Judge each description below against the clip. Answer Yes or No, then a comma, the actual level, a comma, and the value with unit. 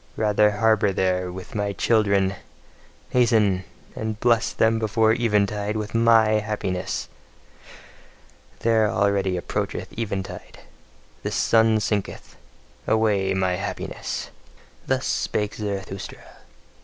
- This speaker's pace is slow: Yes, slow, 100 wpm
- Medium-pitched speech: No, low, 105 Hz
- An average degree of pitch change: No, narrow, 2.2 semitones